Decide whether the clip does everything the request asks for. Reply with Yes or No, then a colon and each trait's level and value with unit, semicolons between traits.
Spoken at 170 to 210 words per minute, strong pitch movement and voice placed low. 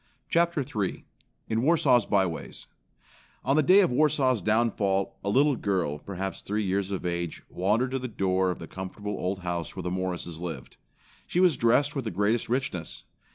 Yes: average, 180 wpm; wide, 5.8 semitones; low, 105 Hz